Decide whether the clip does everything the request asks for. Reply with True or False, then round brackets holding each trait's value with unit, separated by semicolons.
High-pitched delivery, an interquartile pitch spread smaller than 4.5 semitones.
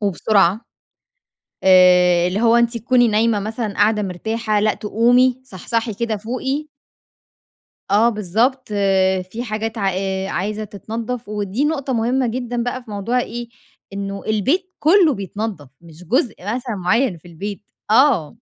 True (220 Hz; 3.5 semitones)